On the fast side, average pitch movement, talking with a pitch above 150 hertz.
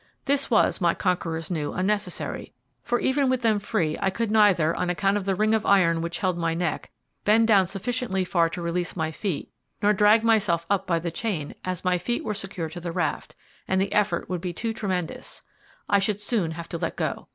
Yes: fast, 215 wpm; average, 3.8 semitones; high, 190 Hz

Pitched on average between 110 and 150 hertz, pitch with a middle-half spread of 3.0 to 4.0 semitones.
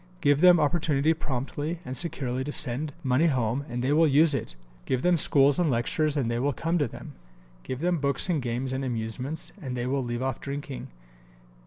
Yes: medium, 140 Hz; average, 3.5 semitones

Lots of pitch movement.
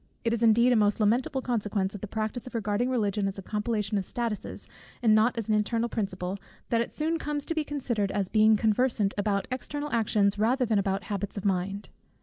No: average, 3.0 semitones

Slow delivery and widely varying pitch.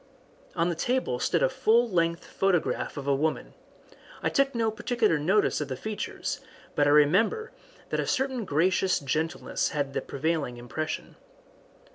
No: average, 155 wpm; wide, 7.0 semitones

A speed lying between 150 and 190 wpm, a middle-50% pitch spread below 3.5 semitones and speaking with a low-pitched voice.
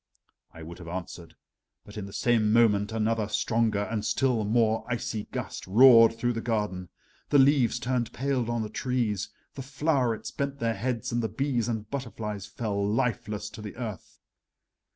Yes: average, 170 wpm; average, 2.8 semitones; low, 115 Hz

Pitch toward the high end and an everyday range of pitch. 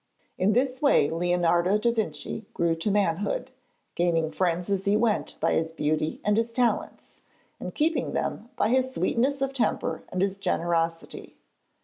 No: high, 200 Hz; wide, 5.8 semitones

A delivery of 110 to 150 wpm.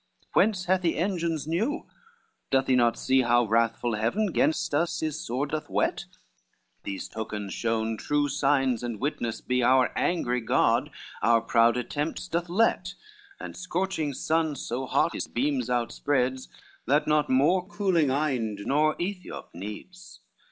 Yes: average, 145 wpm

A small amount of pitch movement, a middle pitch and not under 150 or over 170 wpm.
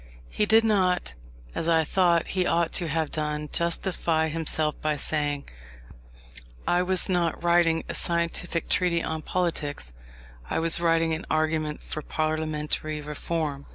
No: narrow, 1.9 semitones; medium, 165 Hz; average, 140 wpm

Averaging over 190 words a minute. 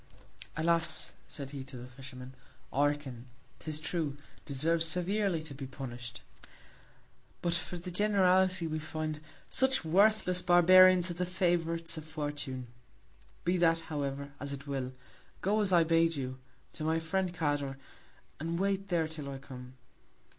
No: average, 145 wpm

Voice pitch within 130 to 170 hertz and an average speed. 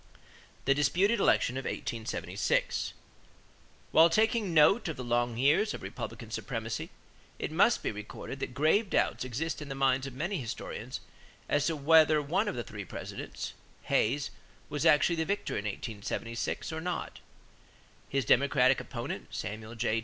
Yes: medium, 140 Hz; average, 155 wpm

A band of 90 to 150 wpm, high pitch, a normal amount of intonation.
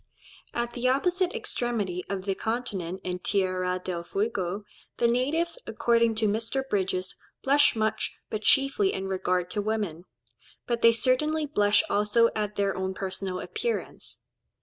Yes: average, 145 wpm; high, 215 Hz; average, 4.8 semitones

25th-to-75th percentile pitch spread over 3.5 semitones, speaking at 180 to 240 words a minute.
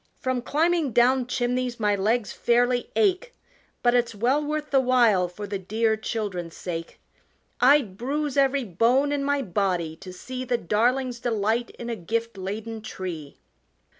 No: average, 4.1 semitones; average, 155 wpm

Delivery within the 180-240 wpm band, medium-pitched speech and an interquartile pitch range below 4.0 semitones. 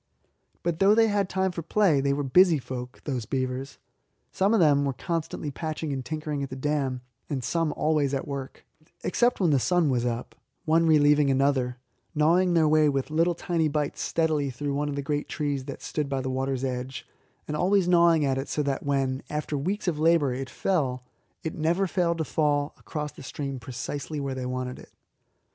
Yes: average, 195 wpm; medium, 145 Hz; average, 3.5 semitones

